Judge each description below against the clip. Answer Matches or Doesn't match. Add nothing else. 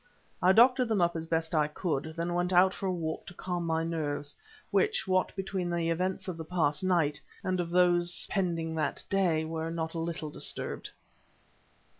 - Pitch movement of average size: Doesn't match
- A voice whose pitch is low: Doesn't match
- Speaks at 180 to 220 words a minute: Matches